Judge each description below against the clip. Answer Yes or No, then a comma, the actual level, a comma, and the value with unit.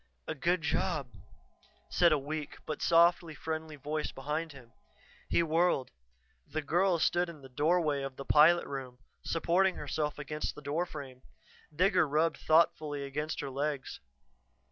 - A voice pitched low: No, medium, 155 Hz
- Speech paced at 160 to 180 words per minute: No, average, 145 wpm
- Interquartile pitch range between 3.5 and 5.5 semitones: No, average, 2.9 semitones